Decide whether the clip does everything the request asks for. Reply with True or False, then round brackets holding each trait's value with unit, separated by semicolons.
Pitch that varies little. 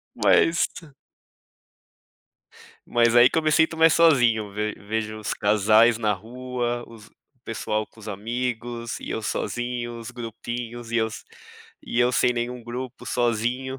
True (2.0 semitones)